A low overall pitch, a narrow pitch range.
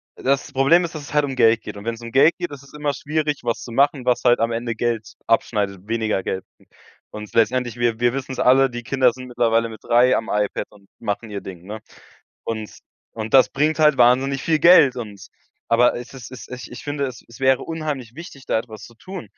No: low, 120 Hz; average, 3.3 semitones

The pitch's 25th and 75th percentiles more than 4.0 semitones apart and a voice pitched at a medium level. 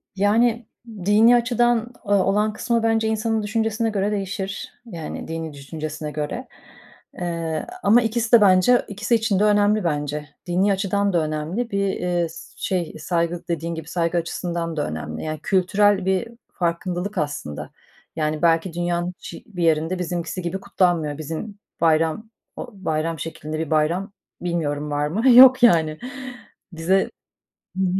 Yes: average, 4.5 semitones; medium, 180 Hz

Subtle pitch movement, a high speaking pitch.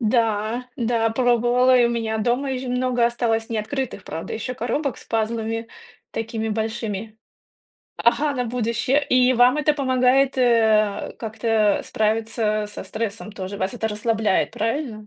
Yes: narrow, 2.3 semitones; high, 230 Hz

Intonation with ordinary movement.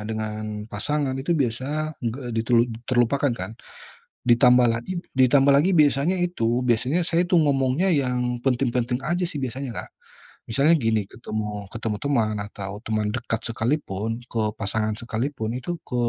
Yes: average, 4.2 semitones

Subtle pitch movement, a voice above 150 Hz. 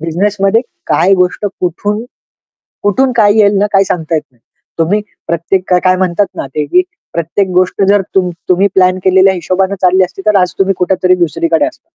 Yes: narrow, 2.2 semitones; medium, 185 Hz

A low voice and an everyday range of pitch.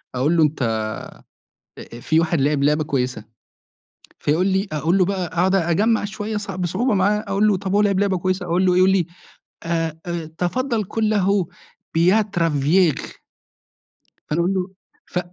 No: medium, 180 Hz; average, 3.5 semitones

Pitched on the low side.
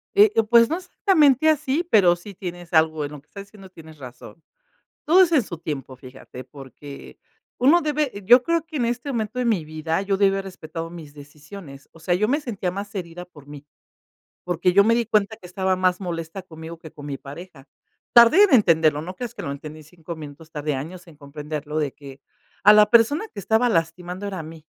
No: medium, 180 Hz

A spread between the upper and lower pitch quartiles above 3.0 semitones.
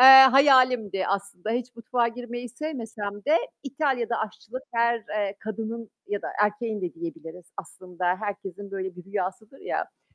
Yes: average, 3.8 semitones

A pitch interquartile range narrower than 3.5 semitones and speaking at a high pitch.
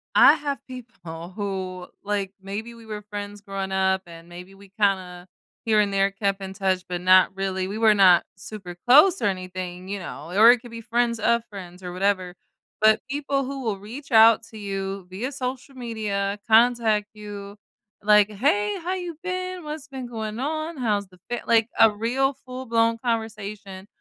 No: average, 3.8 semitones; high, 210 Hz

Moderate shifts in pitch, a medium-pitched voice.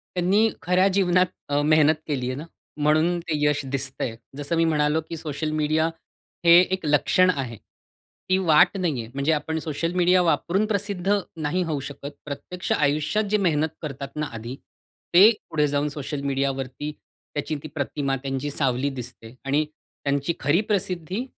Yes: average, 3.9 semitones; medium, 155 Hz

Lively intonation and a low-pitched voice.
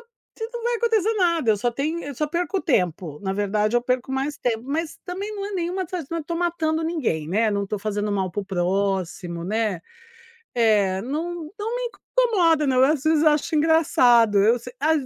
No: wide, 8.4 semitones; very high, 265 Hz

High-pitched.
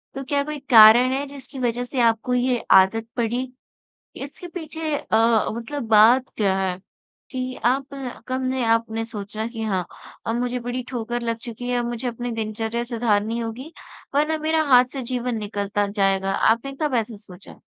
Yes: high, 235 Hz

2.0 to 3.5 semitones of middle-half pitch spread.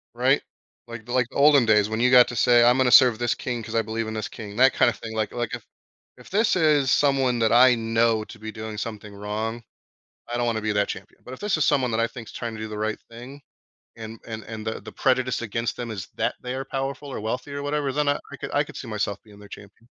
Yes: average, 2.9 semitones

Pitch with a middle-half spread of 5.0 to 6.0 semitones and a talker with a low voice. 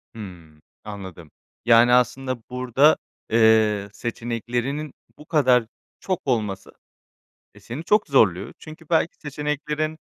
Yes: wide, 5.5 semitones; low, 125 Hz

